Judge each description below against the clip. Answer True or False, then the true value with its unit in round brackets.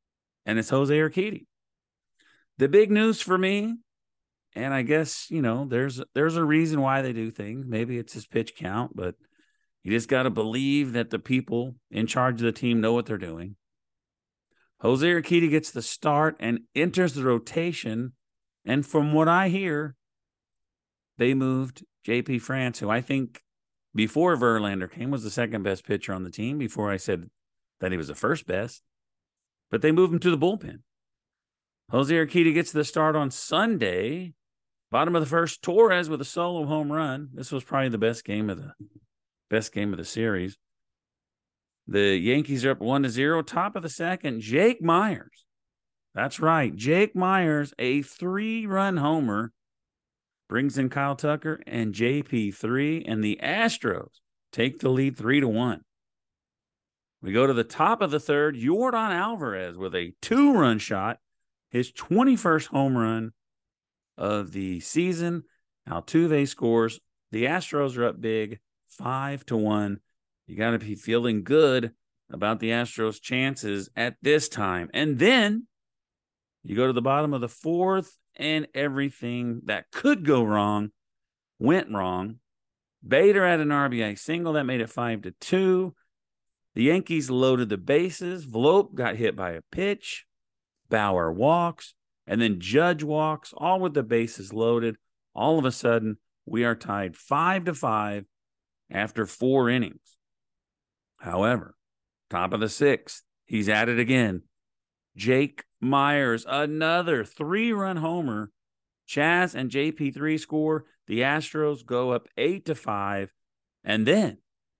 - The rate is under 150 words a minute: False (155 wpm)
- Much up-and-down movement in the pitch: True (5.9 semitones)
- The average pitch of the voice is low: True (130 Hz)